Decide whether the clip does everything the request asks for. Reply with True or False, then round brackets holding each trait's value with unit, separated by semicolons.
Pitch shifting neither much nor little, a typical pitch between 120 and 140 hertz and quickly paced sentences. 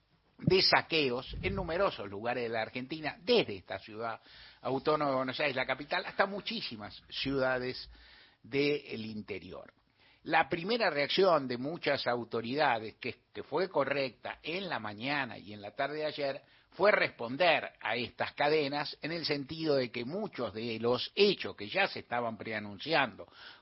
False (4.7 semitones; 135 Hz; 150 wpm)